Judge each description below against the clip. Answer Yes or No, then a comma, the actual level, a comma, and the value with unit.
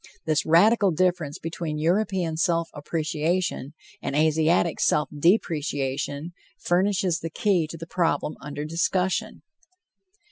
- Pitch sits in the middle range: Yes, medium, 165 Hz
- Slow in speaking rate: Yes, slow, 110 wpm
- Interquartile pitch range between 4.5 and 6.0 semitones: No, average, 2.9 semitones